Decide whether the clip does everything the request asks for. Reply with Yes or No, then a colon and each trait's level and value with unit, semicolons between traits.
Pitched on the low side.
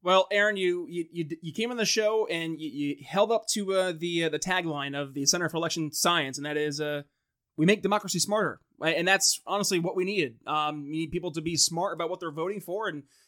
No: medium, 170 Hz